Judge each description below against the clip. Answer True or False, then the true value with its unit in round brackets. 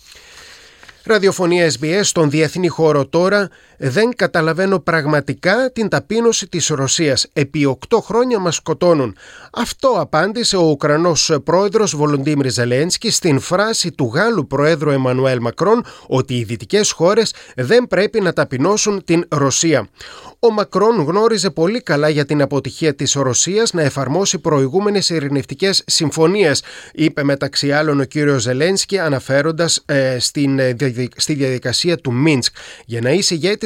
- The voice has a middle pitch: True (160 Hz)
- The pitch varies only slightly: False (5.5 semitones)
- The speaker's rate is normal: True (135 wpm)